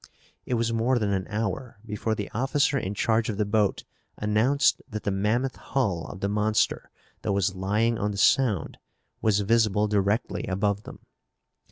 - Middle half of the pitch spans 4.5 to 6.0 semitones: No, narrow, 2.5 semitones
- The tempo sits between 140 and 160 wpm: No, average, 170 wpm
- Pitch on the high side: No, low, 105 Hz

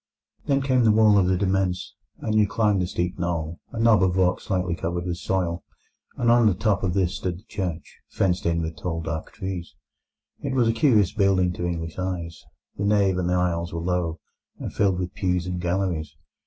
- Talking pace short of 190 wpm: No, average, 195 wpm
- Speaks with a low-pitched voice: Yes, very low, 90 Hz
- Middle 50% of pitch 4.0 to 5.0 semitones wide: No, average, 2.7 semitones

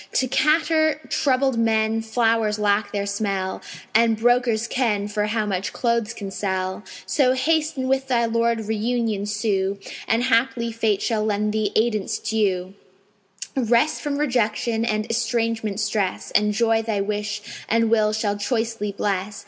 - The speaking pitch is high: Yes, high, 220 Hz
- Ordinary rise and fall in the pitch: No, narrow, 2.2 semitones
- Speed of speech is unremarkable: Yes, average, 150 wpm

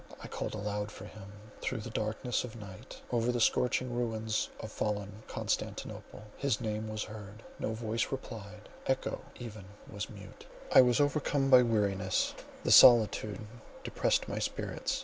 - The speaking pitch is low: Yes, low, 110 Hz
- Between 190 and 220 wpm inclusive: No, average, 145 wpm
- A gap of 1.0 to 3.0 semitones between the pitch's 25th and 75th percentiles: Yes, narrow, 2.6 semitones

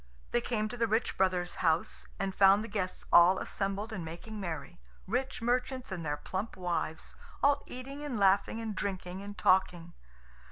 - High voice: Yes, high, 195 Hz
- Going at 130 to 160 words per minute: No, average, 170 wpm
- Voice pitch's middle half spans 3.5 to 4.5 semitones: Yes, average, 4.1 semitones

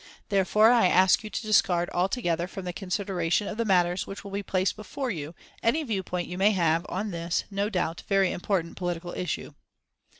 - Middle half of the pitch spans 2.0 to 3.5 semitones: Yes, average, 2.7 semitones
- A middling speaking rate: Yes, average, 190 wpm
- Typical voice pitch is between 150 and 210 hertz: Yes, high, 190 Hz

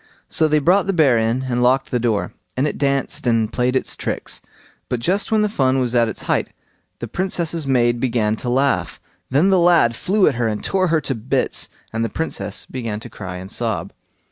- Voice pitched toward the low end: Yes, low, 130 Hz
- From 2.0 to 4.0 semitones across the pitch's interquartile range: No, wide, 5.4 semitones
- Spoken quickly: Yes, fast, 215 wpm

